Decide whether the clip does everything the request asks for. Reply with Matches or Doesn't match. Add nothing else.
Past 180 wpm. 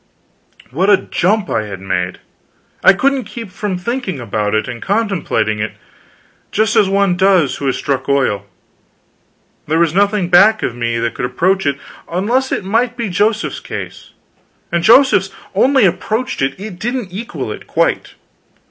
Doesn't match